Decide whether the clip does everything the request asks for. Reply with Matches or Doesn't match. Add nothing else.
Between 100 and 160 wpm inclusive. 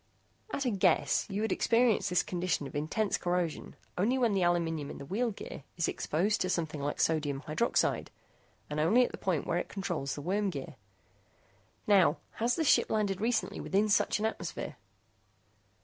Doesn't match